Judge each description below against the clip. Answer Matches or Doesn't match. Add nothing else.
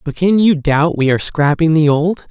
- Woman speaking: Doesn't match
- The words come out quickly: Matches